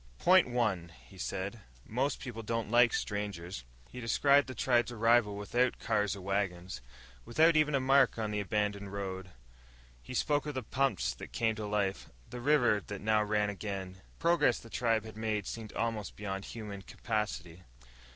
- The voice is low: Yes, low, 110 Hz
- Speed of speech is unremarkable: Yes, average, 170 wpm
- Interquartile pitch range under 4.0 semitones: Yes, average, 3.3 semitones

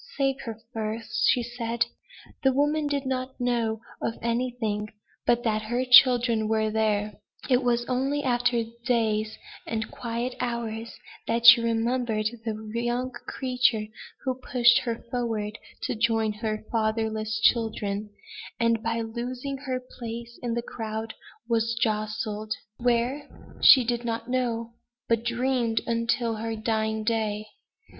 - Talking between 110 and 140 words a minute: Yes, slow, 135 wpm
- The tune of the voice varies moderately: No, narrow, 2.1 semitones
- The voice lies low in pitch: No, high, 230 Hz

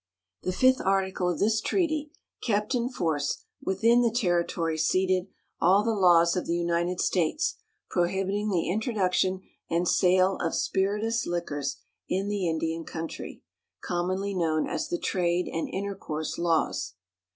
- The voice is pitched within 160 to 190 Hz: Yes, medium, 185 Hz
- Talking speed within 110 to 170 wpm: Yes, average, 140 wpm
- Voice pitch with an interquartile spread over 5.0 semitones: No, average, 3.1 semitones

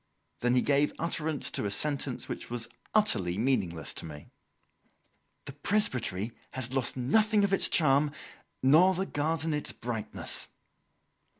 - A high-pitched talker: No, medium, 140 Hz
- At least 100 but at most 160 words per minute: Yes, slow, 135 wpm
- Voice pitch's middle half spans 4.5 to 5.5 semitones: Yes, average, 5.2 semitones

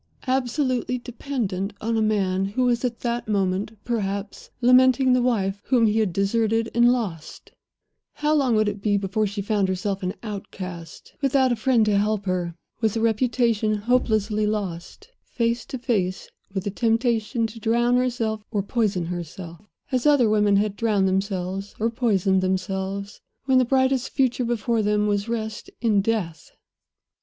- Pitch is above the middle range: Yes, high, 215 Hz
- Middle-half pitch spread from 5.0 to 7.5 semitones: No, average, 3.4 semitones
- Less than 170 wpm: Yes, average, 160 wpm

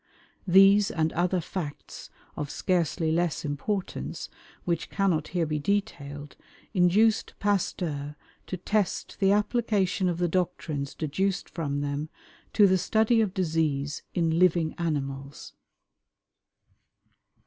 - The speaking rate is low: Yes, slow, 115 wpm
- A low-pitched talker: No, medium, 175 Hz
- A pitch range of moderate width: Yes, average, 4.3 semitones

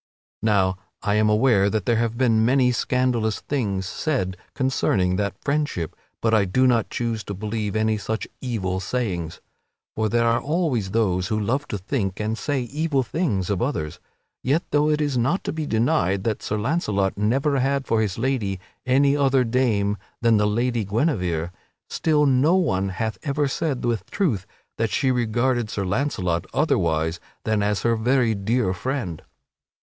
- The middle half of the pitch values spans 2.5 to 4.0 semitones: No, average, 4.8 semitones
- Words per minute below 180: Yes, average, 170 wpm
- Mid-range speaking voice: No, low, 115 Hz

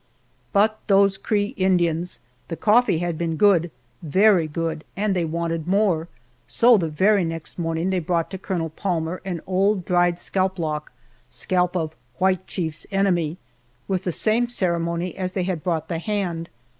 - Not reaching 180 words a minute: Yes, average, 160 wpm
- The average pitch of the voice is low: No, medium, 180 Hz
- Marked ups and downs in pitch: No, average, 2.8 semitones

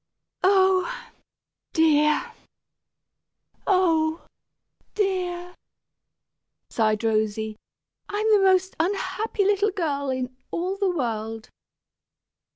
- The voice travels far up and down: Yes, wide, 6.9 semitones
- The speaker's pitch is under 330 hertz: No, very high, 350 Hz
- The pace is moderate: No, slow, 75 wpm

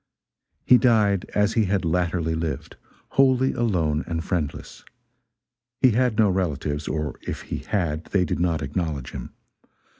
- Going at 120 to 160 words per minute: Yes, average, 145 wpm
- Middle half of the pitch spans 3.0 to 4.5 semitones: No, average, 5.1 semitones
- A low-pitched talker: Yes, very low, 90 Hz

